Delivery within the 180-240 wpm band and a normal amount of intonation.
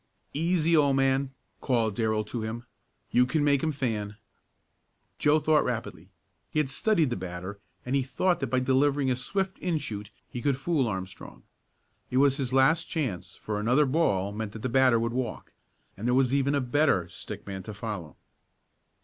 Yes: average, 185 wpm; average, 4.9 semitones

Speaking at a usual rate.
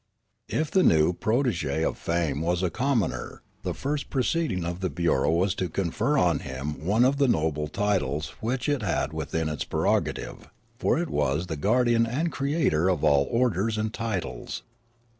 Yes: average, 170 wpm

